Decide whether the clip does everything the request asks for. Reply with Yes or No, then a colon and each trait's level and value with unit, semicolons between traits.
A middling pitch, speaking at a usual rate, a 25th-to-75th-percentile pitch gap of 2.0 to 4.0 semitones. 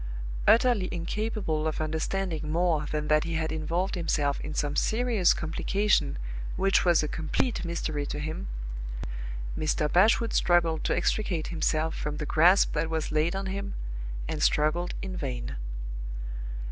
Yes: medium, 165 Hz; average, 145 wpm; average, 3.7 semitones